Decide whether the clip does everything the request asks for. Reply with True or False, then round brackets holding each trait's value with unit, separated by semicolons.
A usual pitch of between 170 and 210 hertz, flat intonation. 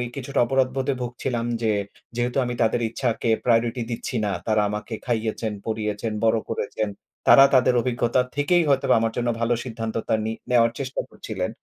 False (120 Hz; 2.3 semitones)